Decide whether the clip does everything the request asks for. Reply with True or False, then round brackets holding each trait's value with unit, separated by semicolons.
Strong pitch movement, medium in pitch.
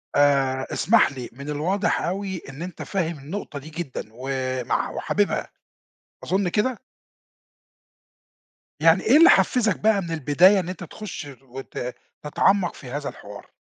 True (6.0 semitones; 165 Hz)